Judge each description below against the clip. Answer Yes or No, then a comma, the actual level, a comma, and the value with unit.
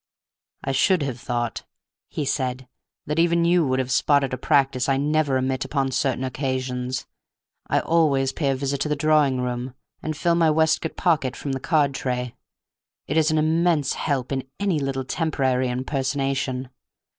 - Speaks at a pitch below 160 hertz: Yes, low, 135 Hz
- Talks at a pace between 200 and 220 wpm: No, average, 170 wpm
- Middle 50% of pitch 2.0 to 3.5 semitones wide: Yes, average, 3.0 semitones